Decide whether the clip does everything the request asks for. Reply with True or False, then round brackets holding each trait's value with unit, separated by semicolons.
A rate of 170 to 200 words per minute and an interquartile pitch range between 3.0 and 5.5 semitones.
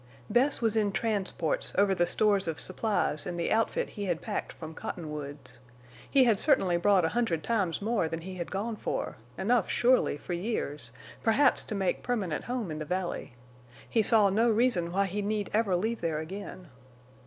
True (185 wpm; 4.7 semitones)